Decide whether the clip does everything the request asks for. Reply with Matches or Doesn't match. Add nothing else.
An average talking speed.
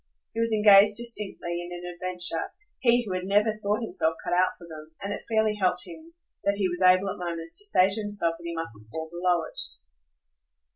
Doesn't match